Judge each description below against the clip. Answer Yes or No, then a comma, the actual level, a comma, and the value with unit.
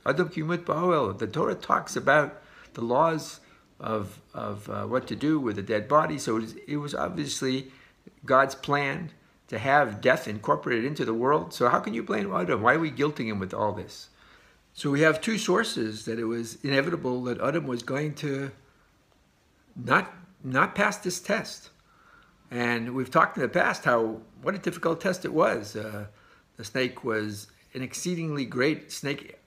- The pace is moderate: Yes, average, 170 wpm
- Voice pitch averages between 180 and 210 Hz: No, low, 135 Hz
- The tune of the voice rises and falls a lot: Yes, wide, 5.8 semitones